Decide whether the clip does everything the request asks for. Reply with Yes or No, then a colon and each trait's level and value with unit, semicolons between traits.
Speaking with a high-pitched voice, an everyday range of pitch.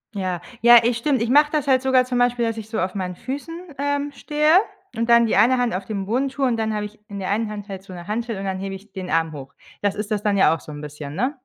Yes: high, 220 Hz; average, 4.7 semitones